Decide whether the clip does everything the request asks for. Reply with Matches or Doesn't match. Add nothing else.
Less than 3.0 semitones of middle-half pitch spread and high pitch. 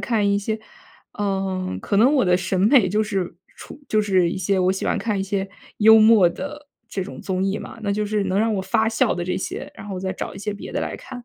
Matches